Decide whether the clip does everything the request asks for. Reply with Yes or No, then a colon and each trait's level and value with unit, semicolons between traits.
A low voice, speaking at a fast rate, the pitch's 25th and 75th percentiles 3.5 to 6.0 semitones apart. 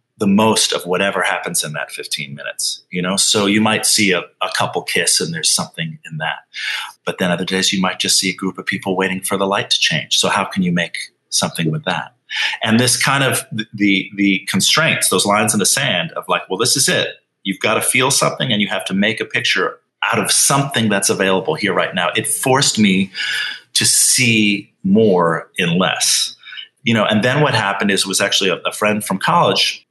No: low, 100 Hz; fast, 225 wpm; average, 2.8 semitones